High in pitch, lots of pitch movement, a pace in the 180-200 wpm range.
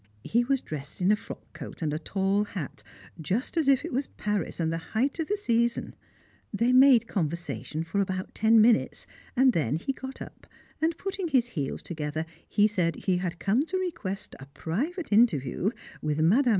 Yes: high, 210 Hz; wide, 7.7 semitones; average, 190 wpm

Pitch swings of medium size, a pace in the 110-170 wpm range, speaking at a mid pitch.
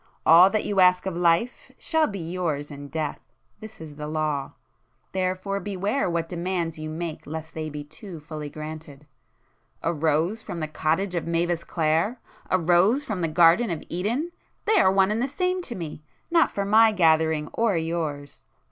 Yes: average, 4.1 semitones; average, 165 wpm; medium, 170 Hz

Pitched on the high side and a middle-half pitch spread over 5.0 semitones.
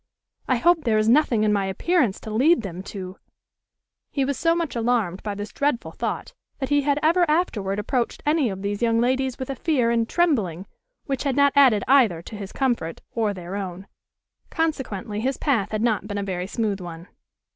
Yes: high, 230 Hz; wide, 5.6 semitones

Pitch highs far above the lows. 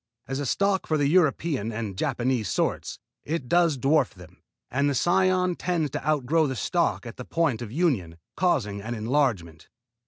Yes: wide, 6.2 semitones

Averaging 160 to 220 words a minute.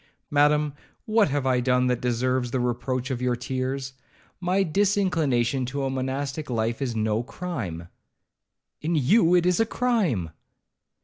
No: average, 145 wpm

